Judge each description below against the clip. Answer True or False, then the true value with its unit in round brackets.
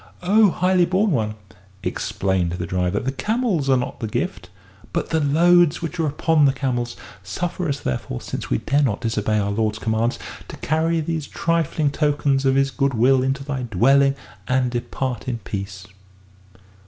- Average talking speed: True (170 wpm)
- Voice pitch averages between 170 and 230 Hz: False (135 Hz)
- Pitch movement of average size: False (6.3 semitones)